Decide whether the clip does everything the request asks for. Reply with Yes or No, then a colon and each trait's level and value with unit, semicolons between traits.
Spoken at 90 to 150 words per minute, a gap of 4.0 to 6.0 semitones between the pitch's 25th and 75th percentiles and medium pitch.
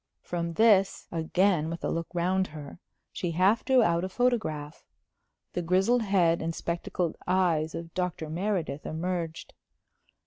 No: average, 140 wpm; narrow, 2.6 semitones; medium, 175 Hz